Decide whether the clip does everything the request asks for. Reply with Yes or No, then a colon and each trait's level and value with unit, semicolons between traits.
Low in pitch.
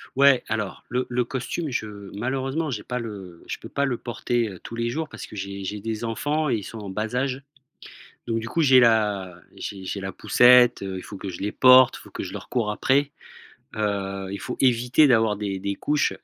Yes: low, 115 Hz